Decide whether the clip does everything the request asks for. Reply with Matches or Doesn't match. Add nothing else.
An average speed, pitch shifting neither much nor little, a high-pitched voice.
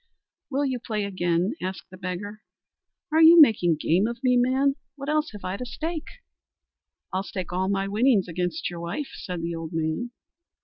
Doesn't match